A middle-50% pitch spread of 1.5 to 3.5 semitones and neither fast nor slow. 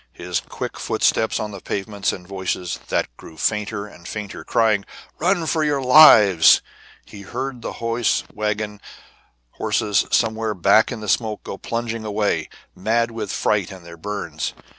Yes: narrow, 2.6 semitones; average, 160 wpm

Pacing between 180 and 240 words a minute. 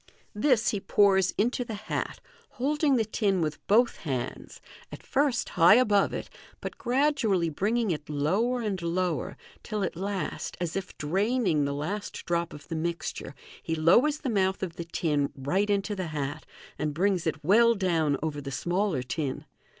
No: average, 170 wpm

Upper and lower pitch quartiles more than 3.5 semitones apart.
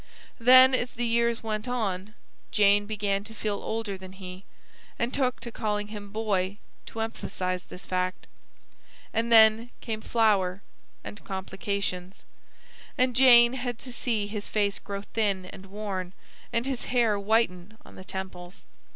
No: average, 3.2 semitones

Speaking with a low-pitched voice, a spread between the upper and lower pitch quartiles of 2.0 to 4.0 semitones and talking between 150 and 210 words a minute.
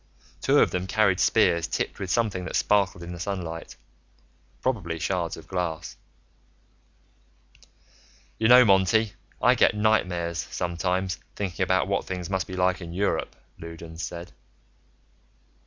No: very low, 90 Hz; narrow, 2.5 semitones; slow, 135 wpm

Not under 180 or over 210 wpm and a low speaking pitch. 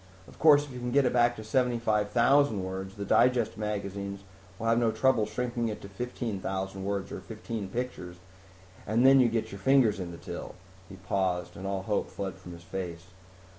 Yes: average, 195 wpm; low, 105 Hz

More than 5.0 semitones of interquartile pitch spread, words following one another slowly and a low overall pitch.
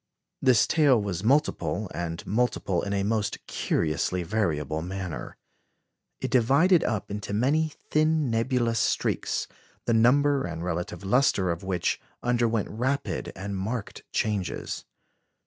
Yes: wide, 5.4 semitones; slow, 125 wpm; low, 110 Hz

